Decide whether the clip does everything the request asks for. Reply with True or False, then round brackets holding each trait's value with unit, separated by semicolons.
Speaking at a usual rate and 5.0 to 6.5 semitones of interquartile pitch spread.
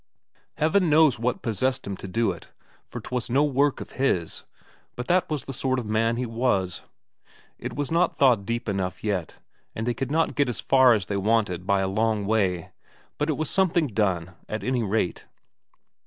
True (195 wpm; 5.3 semitones)